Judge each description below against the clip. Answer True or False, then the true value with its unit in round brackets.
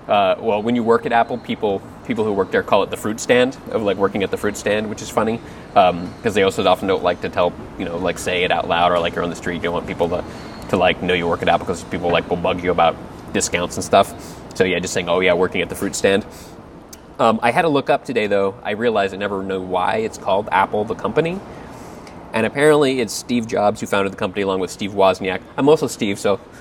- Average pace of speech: False (265 wpm)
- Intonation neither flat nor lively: True (3.4 semitones)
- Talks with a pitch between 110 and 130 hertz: False (100 Hz)